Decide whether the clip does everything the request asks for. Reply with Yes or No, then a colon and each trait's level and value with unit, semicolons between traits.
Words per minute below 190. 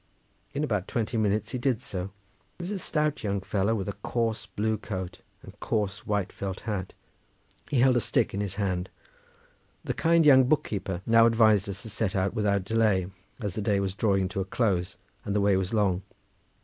No: average, 200 wpm